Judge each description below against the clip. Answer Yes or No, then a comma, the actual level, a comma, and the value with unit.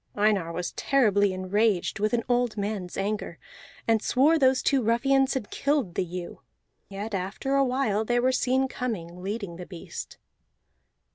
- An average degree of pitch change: Yes, average, 4.8 semitones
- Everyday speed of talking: Yes, average, 155 wpm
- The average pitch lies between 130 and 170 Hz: No, high, 215 Hz